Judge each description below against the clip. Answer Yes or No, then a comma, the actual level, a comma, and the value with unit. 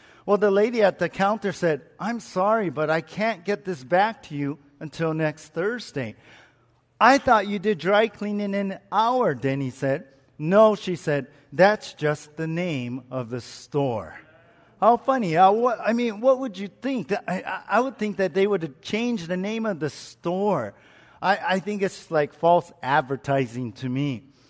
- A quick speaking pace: No, average, 170 wpm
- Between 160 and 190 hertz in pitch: Yes, medium, 185 Hz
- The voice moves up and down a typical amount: No, wide, 6.3 semitones